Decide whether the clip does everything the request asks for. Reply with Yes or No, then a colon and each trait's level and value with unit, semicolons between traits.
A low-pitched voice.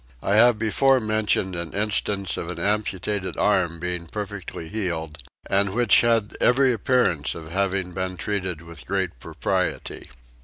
Yes: very low, 95 Hz